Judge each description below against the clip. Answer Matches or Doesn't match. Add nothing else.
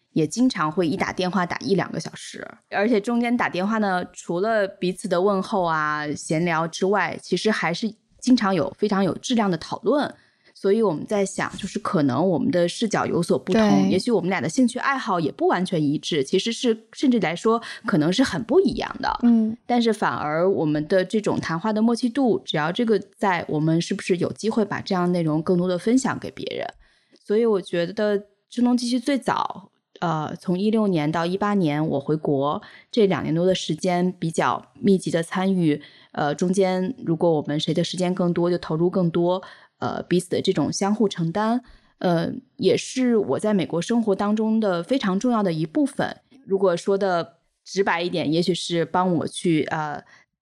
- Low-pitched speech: Doesn't match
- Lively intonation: Doesn't match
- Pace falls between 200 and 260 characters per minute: Doesn't match